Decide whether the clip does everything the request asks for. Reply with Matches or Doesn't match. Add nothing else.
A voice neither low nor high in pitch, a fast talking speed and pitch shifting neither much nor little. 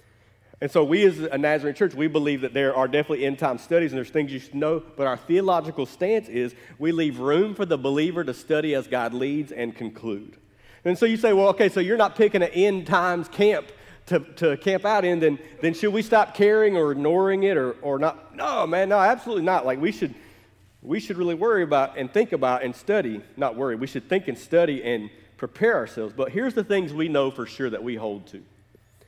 Doesn't match